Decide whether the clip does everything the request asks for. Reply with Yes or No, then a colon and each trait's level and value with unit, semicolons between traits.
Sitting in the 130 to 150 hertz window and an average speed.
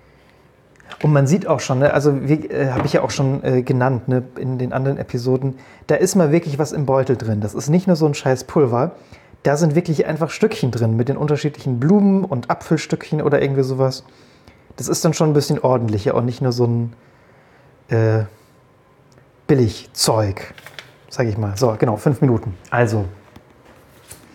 Yes: low, 135 Hz; average, 175 wpm